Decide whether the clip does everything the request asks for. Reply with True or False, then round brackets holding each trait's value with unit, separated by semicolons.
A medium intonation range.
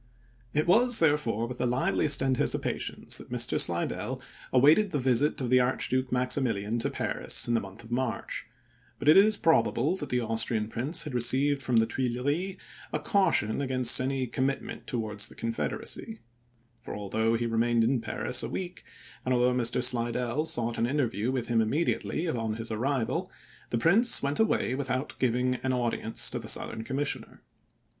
True (3.6 semitones)